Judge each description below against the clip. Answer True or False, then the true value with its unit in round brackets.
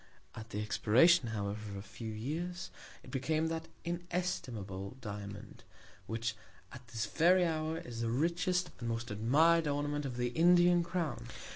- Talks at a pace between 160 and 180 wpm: False (150 wpm)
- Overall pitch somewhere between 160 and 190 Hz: False (130 Hz)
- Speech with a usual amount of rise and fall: False (7.0 semitones)